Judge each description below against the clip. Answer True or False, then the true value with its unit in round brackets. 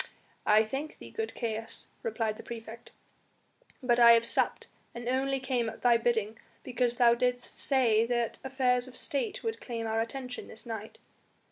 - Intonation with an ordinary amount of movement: False (2.3 semitones)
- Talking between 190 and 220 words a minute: False (165 wpm)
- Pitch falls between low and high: False (240 Hz)